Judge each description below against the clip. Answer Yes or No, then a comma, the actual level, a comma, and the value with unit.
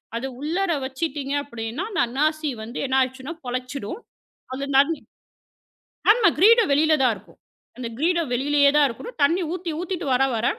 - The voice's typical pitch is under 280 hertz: No, very high, 285 Hz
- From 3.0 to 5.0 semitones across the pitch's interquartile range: Yes, average, 4.5 semitones